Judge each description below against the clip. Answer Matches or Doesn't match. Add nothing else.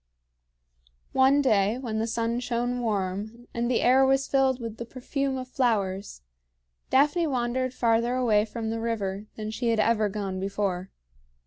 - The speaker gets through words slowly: Doesn't match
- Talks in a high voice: Matches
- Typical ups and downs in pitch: Matches